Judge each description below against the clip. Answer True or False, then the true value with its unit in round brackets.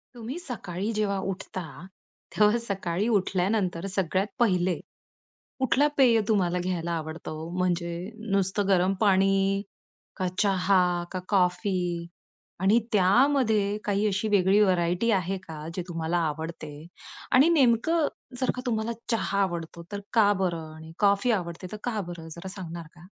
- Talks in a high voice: True (195 Hz)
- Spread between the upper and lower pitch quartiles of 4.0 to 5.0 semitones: False (3.5 semitones)